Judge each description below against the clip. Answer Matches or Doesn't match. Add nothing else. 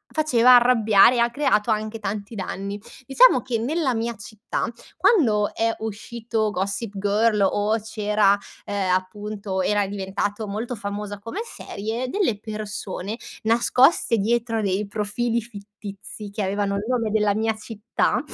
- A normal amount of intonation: Doesn't match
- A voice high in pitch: Matches